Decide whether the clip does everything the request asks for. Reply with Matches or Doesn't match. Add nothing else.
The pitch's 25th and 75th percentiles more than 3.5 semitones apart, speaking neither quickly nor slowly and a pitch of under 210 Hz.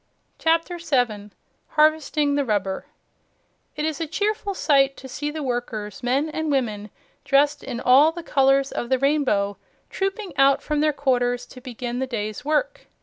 Doesn't match